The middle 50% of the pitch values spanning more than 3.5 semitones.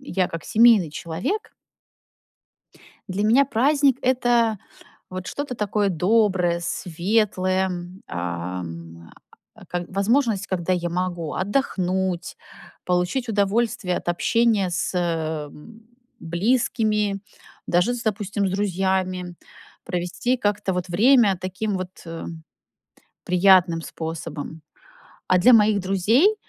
Yes: average, 4.0 semitones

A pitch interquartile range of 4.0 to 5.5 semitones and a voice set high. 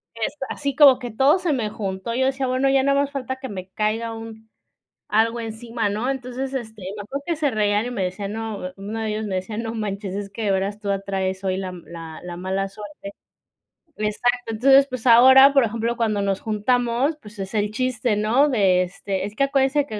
Yes: average, 4.3 semitones; high, 220 Hz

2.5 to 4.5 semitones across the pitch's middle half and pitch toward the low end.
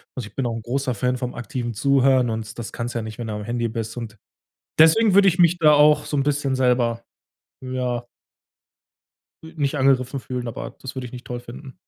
Yes: average, 2.8 semitones; low, 125 Hz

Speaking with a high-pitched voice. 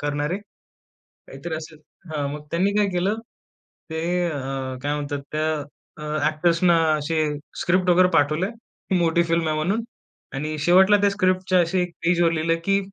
No: medium, 165 Hz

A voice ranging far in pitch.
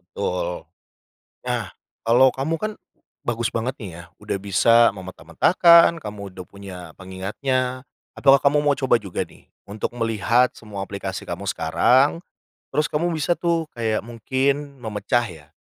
Yes: wide, 5.8 semitones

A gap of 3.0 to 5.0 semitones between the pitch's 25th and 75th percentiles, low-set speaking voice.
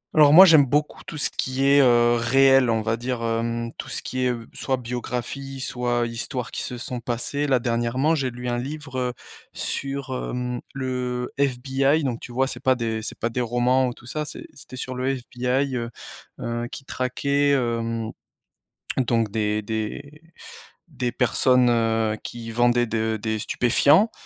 No: narrow, 2.4 semitones; low, 125 Hz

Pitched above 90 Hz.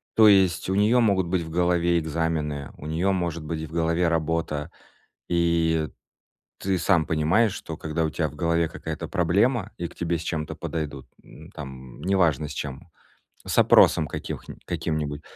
No: very low, 85 Hz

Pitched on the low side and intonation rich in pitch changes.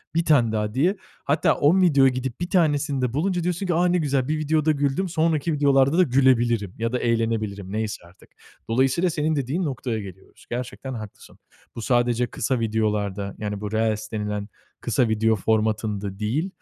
Yes: low, 125 Hz; wide, 5.7 semitones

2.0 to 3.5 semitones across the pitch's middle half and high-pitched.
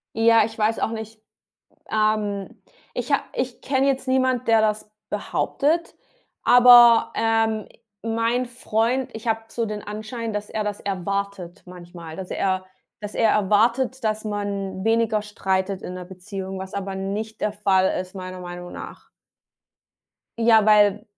Yes: average, 2.8 semitones; high, 215 Hz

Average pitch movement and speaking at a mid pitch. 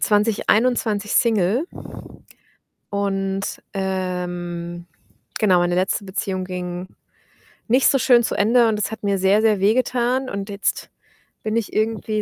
No: average, 3.1 semitones; high, 205 Hz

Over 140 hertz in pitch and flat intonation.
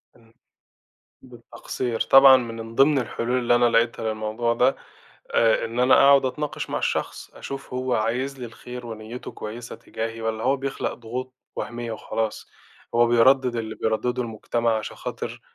No: low, 120 Hz; narrow, 2.1 semitones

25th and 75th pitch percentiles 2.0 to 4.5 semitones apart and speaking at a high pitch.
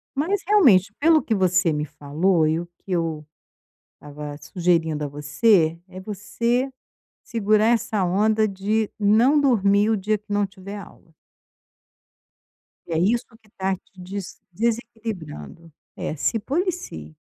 No: average, 5.0 semitones; high, 200 Hz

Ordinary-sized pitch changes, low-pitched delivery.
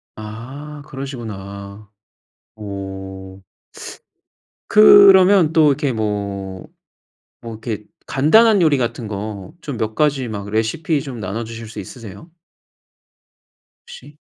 No: wide, 6.6 semitones; low, 115 Hz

